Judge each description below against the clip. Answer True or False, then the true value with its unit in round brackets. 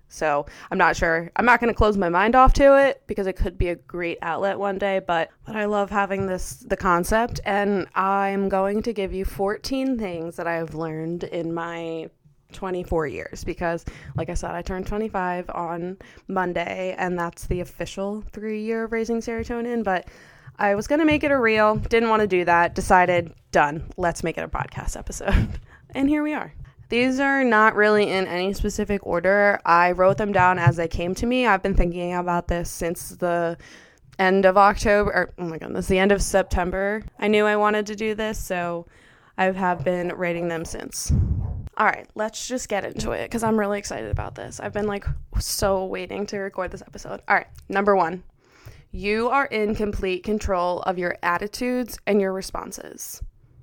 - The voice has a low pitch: False (190 Hz)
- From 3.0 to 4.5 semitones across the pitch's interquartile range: True (3.4 semitones)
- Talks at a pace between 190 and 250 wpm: True (195 wpm)